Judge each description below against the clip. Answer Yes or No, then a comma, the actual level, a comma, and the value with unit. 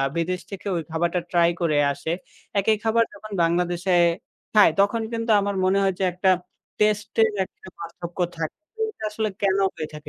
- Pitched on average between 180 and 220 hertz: Yes, high, 190 Hz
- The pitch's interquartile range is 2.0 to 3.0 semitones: No, average, 3.7 semitones